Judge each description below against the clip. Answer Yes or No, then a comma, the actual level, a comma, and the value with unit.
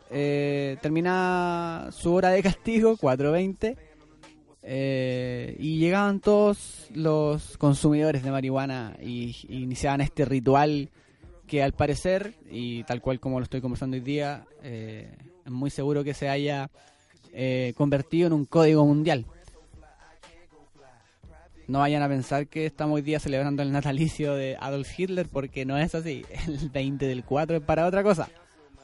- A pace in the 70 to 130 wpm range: No, average, 150 wpm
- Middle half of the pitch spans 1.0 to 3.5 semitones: Yes, average, 2.9 semitones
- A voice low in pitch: No, medium, 145 Hz